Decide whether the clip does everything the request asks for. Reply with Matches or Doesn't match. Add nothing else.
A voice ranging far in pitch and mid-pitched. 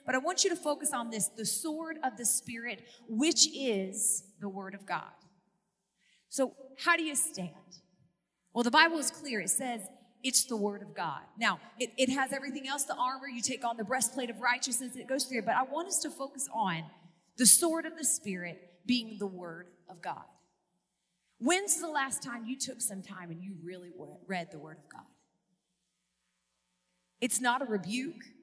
Doesn't match